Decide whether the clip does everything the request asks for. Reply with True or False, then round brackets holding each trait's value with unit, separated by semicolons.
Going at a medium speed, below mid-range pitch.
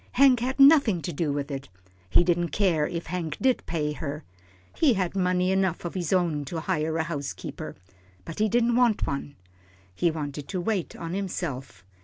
False (185 wpm; 175 Hz)